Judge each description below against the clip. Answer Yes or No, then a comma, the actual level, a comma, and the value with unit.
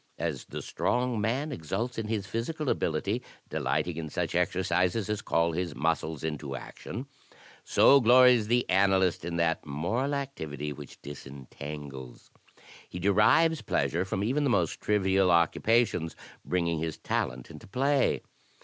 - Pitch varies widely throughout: Yes, wide, 6.9 semitones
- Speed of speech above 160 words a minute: No, average, 140 wpm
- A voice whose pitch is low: Yes, very low, 95 Hz